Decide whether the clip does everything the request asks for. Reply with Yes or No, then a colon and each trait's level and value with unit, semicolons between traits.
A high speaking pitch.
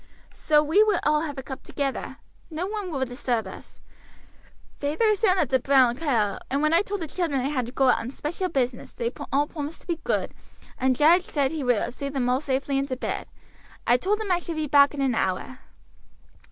Yes: very high, 280 Hz